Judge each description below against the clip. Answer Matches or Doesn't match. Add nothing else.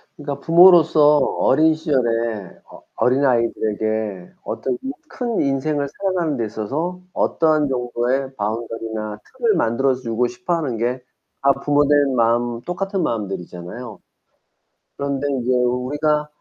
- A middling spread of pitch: Matches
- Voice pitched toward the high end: Doesn't match